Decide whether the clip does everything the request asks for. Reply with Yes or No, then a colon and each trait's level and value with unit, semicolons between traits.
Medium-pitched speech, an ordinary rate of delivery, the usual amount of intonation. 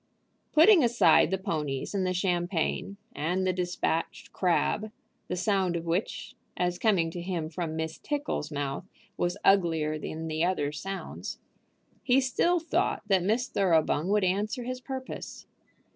Yes: medium, 180 Hz; average, 145 wpm; average, 4.3 semitones